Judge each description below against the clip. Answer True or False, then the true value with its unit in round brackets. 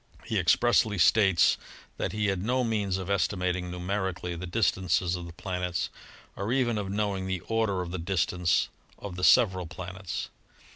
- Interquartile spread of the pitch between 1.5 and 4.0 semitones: True (2.5 semitones)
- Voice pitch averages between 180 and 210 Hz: False (95 Hz)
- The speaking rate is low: False (165 wpm)